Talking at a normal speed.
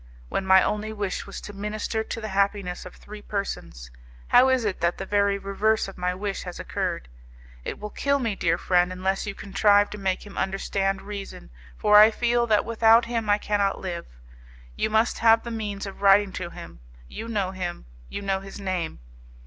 Yes: average, 195 wpm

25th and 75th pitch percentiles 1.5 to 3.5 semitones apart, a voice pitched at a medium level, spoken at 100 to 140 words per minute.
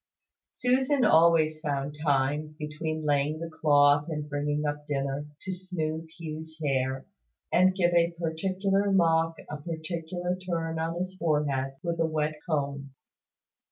Yes: narrow, 2.6 semitones; medium, 160 Hz; slow, 135 wpm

